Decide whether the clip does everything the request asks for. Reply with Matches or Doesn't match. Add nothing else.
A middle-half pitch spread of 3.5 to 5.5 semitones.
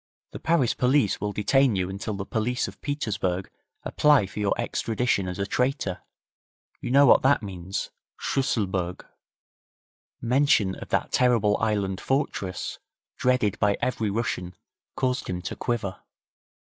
Matches